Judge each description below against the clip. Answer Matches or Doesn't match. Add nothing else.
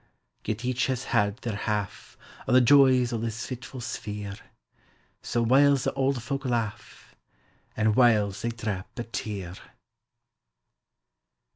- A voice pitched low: Matches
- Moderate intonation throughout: Matches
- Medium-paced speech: Doesn't match